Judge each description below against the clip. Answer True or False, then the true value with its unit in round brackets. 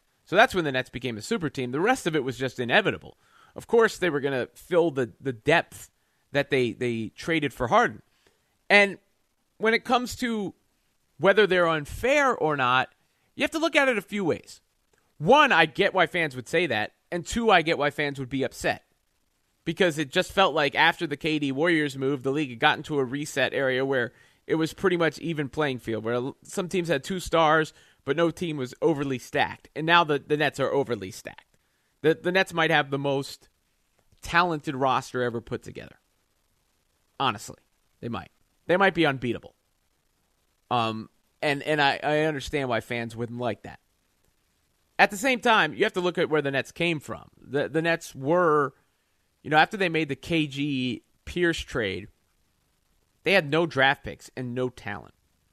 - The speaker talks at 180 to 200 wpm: True (195 wpm)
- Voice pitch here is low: False (150 Hz)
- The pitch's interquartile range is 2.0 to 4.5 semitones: False (5.0 semitones)